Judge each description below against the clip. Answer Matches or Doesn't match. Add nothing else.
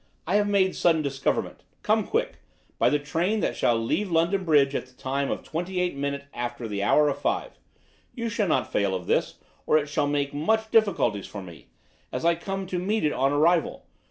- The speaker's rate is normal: Doesn't match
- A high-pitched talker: Doesn't match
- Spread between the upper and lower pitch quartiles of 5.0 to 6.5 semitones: Matches